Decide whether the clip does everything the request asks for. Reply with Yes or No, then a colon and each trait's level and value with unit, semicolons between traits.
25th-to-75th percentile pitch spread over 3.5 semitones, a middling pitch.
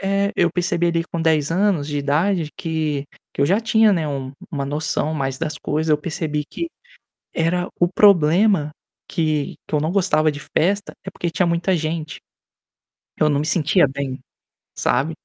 No: average, 3.1 semitones; medium, 160 Hz